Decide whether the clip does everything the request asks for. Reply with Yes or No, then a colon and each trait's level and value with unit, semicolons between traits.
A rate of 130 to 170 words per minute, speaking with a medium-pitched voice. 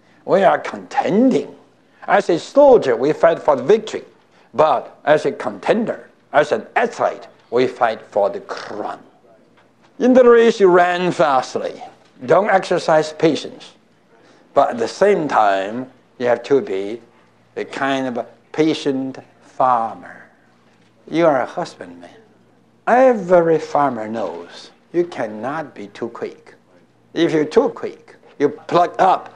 Yes: slow, 135 wpm; medium, 170 Hz